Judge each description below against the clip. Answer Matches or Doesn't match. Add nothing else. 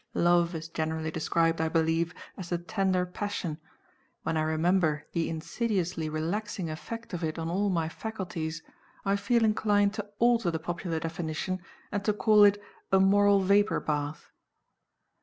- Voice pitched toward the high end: Doesn't match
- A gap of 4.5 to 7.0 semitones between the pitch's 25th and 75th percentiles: Doesn't match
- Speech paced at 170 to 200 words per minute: Doesn't match